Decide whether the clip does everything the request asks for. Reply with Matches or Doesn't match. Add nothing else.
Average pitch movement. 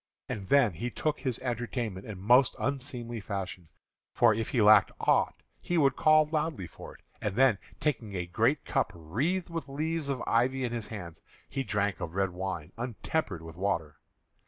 Doesn't match